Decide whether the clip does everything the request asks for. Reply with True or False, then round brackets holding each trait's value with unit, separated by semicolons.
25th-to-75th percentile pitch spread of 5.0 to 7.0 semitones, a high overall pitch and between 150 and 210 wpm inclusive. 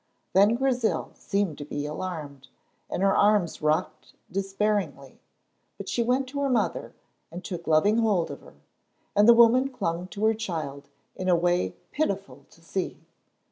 True (5.5 semitones; 195 Hz; 160 wpm)